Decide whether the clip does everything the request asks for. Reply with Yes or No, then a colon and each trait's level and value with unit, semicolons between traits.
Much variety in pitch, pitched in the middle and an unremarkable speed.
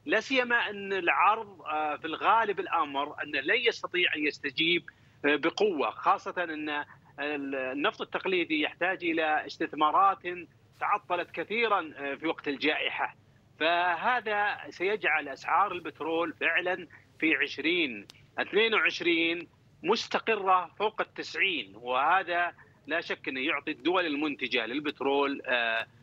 Yes: wide, 5.8 semitones; medium, 170 Hz; average, 100 wpm